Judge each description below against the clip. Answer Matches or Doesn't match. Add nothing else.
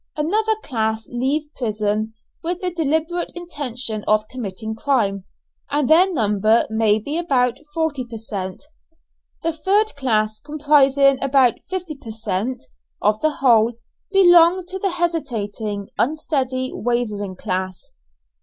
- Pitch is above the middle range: Matches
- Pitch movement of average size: Doesn't match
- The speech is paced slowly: Matches